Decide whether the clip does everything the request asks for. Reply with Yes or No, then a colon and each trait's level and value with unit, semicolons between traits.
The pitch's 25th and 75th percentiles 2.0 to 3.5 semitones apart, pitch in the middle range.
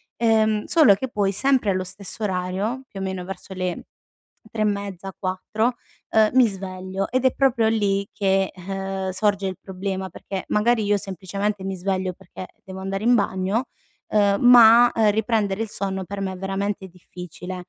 No: narrow, 2.4 semitones; high, 195 Hz